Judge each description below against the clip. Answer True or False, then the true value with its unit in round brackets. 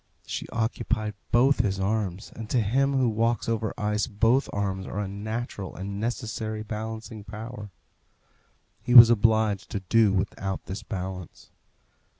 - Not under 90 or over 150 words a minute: True (145 wpm)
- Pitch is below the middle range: True (110 Hz)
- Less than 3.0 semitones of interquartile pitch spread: True (2.4 semitones)